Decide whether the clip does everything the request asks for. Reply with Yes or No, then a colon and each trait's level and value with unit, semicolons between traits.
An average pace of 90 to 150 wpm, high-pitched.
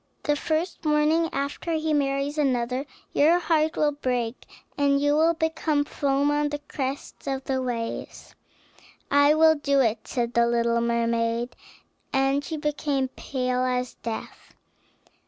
Yes: average, 140 wpm; very high, 280 Hz